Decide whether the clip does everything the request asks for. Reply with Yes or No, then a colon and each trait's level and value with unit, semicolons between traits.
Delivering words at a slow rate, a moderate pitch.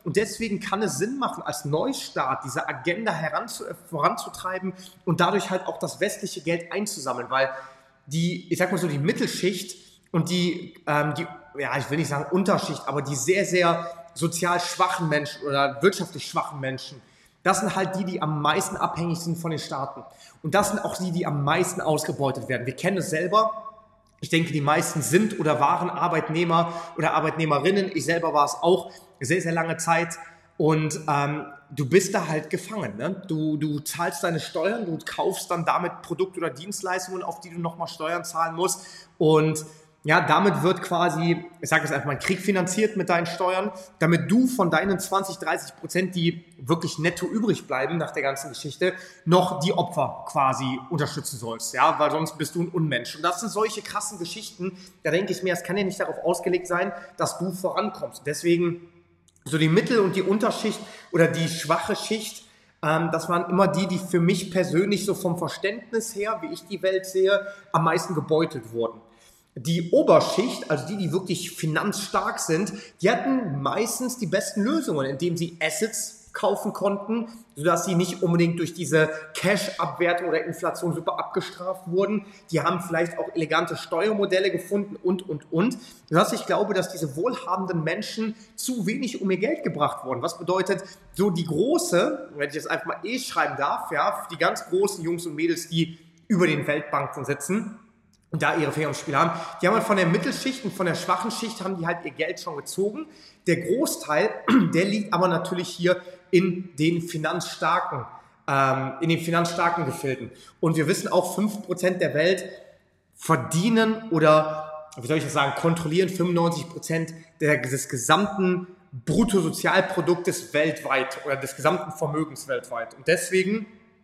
No: average, 175 wpm; medium, 175 Hz